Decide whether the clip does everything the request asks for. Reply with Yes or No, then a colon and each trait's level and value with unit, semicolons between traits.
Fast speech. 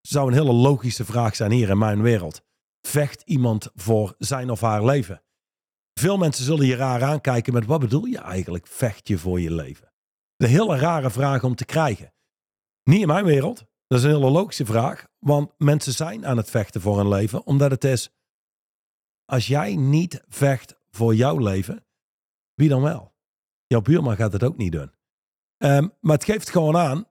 No: average, 190 wpm